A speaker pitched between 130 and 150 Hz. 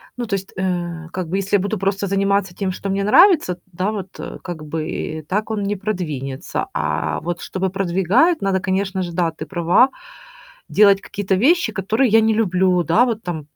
No: high, 190 Hz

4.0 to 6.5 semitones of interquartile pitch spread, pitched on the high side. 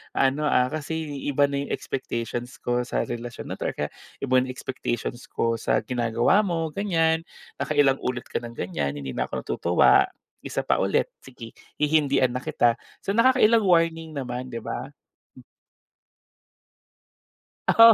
No: average, 5.1 semitones; low, 130 Hz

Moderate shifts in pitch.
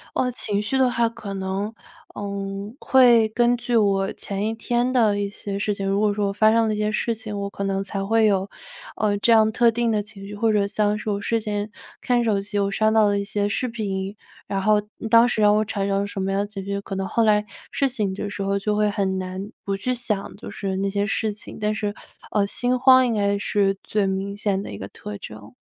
No: narrow, 1.9 semitones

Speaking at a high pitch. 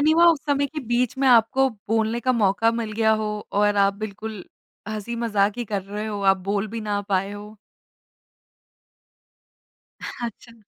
Yes: high, 220 Hz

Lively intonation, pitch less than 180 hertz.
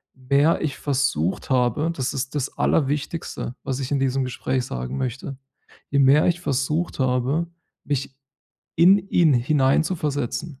No: average, 2.7 semitones; low, 135 Hz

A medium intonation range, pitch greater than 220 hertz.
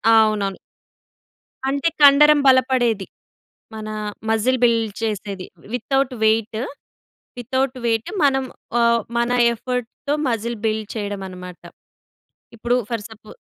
Yes: average, 3.1 semitones; high, 230 Hz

